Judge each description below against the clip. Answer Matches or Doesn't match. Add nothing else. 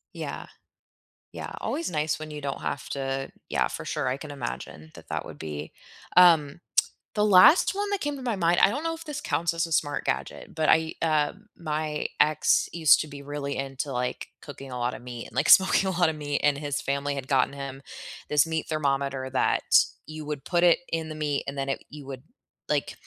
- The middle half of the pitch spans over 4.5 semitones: Doesn't match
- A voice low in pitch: Doesn't match